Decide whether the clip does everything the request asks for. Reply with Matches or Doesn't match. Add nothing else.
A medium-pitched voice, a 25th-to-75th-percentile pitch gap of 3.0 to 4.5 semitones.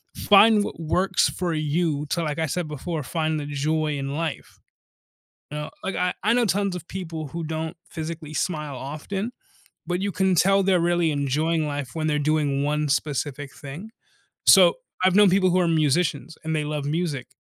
Matches